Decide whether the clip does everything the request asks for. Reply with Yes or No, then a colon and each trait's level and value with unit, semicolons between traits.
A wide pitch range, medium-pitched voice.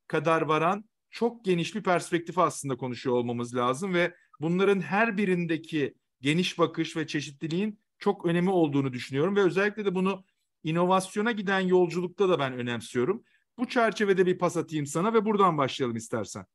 No: average, 4.6 semitones; medium, 175 Hz